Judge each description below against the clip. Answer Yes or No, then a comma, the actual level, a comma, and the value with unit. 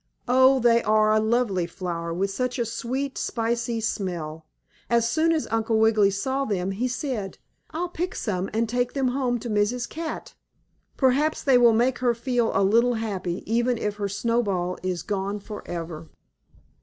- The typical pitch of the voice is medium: No, high, 225 Hz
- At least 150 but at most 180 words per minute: Yes, average, 170 wpm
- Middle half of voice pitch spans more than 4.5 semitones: No, average, 4.0 semitones